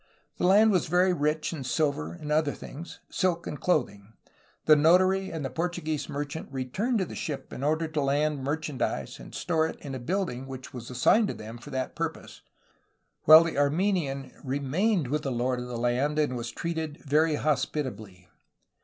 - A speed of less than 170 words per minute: No, average, 185 wpm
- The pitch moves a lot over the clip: No, average, 4.1 semitones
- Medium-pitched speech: Yes, medium, 150 Hz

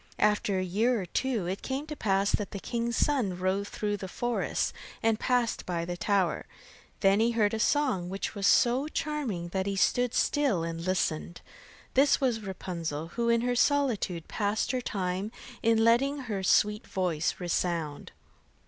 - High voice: Yes, high, 205 Hz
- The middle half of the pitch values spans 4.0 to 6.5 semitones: Yes, average, 4.6 semitones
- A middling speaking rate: Yes, average, 170 wpm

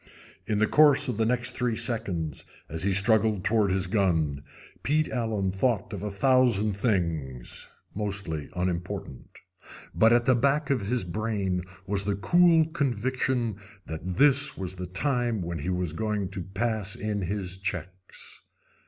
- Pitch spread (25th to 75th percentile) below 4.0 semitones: No, average, 4.6 semitones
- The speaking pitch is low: Yes, low, 105 Hz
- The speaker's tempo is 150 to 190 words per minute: Yes, average, 155 wpm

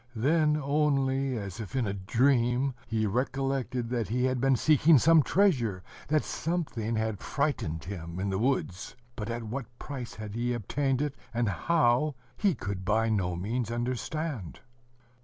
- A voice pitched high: No, low, 120 Hz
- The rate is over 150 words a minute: Yes, average, 160 wpm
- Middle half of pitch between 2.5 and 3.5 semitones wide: No, average, 4.3 semitones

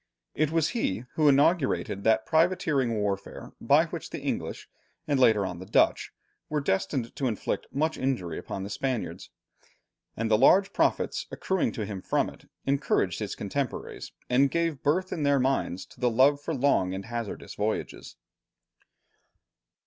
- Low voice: Yes, low, 130 Hz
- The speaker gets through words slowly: No, average, 155 wpm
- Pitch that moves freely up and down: Yes, wide, 5.9 semitones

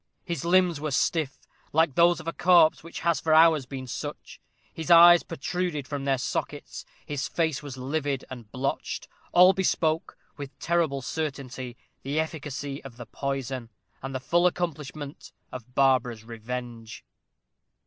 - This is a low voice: No, medium, 145 Hz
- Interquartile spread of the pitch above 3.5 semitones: Yes, average, 4.0 semitones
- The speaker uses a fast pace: No, average, 150 wpm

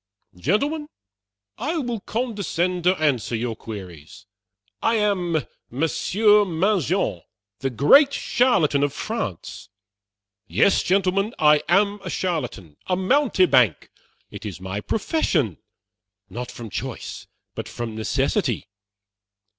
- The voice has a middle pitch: Yes, medium, 175 Hz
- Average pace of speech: No, slow, 105 wpm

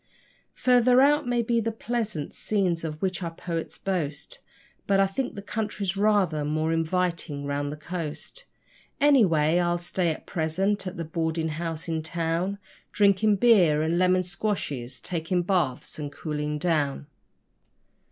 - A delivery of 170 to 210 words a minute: No, average, 145 wpm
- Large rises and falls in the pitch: No, average, 4.2 semitones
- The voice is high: No, medium, 175 Hz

